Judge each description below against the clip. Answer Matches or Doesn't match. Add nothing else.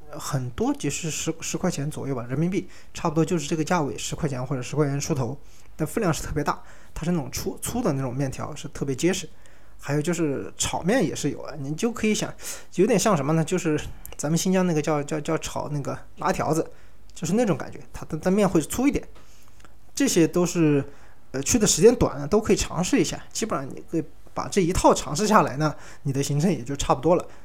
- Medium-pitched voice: Matches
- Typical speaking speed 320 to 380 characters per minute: Matches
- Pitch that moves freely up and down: Doesn't match